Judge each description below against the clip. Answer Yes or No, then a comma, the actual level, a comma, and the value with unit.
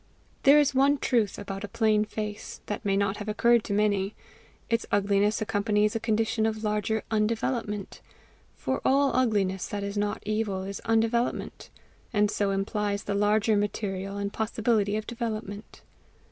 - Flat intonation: Yes, narrow, 1.7 semitones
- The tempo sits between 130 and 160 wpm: Yes, average, 155 wpm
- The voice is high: Yes, high, 210 Hz